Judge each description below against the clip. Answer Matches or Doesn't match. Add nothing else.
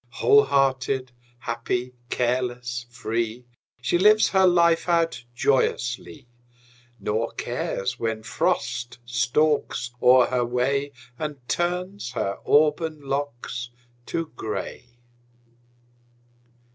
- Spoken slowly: Matches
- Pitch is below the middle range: Matches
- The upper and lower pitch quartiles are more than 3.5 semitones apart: Matches